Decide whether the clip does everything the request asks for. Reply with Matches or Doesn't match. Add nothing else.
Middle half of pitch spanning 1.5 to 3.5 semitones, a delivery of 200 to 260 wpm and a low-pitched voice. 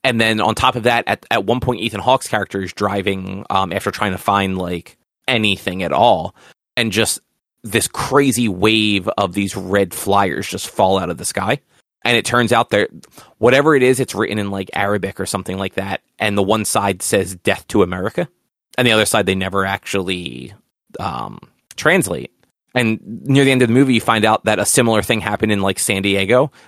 Matches